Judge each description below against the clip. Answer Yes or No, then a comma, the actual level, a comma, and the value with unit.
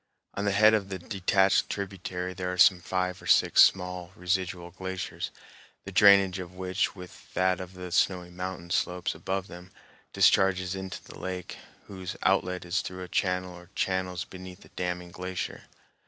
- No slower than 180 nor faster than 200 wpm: No, average, 170 wpm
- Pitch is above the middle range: No, very low, 90 Hz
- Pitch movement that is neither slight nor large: No, narrow, 0.9 semitones